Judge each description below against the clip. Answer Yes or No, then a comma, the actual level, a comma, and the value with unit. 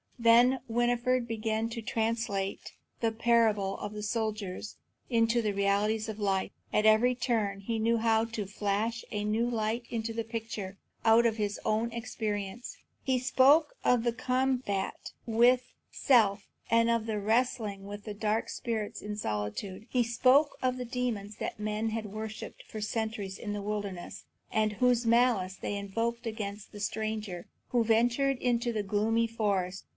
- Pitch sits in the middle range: No, high, 220 Hz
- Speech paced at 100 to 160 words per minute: Yes, average, 155 wpm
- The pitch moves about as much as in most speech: No, narrow, 2.3 semitones